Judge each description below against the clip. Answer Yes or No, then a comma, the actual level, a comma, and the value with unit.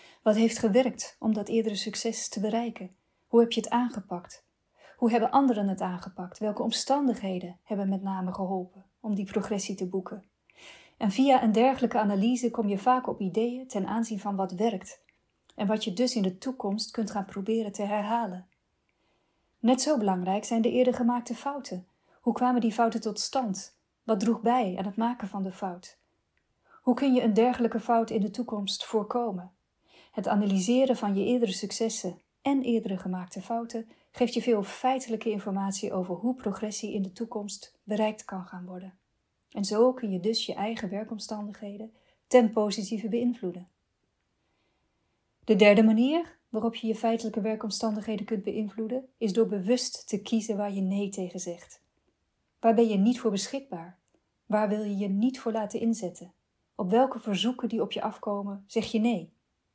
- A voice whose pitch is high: Yes, high, 220 Hz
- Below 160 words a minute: No, average, 170 wpm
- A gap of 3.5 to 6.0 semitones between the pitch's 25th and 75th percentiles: No, average, 2.8 semitones